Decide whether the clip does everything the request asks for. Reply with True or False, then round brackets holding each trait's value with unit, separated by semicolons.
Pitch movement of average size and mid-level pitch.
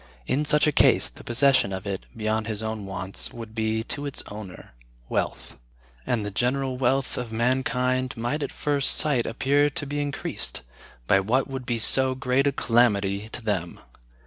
False (3.9 semitones; 120 Hz)